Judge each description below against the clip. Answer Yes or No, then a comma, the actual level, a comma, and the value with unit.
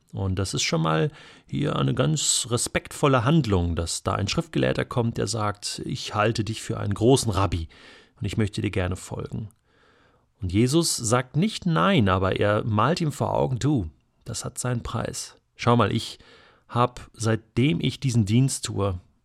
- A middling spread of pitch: Yes, average, 4.6 semitones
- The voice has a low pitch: Yes, low, 115 Hz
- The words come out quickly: No, average, 170 wpm